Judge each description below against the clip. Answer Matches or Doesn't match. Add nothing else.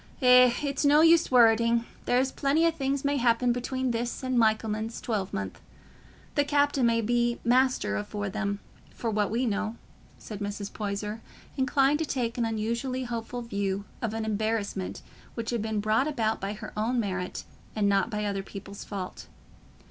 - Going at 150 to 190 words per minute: Matches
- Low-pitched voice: Doesn't match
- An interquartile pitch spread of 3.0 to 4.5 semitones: Matches